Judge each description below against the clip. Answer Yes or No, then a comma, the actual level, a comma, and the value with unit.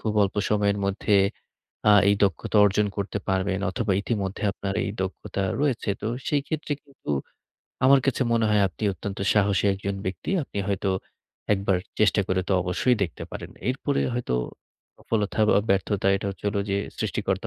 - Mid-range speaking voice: No, low, 100 Hz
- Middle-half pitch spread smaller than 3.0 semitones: Yes, narrow, 2.4 semitones